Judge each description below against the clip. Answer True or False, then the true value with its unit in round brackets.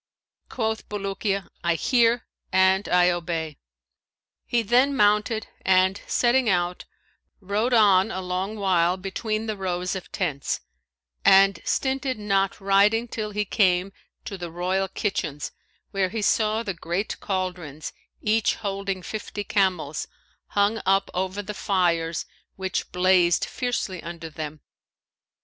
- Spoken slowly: True (125 wpm)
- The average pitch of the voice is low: False (195 Hz)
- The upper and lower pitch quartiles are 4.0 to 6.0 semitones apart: False (2.8 semitones)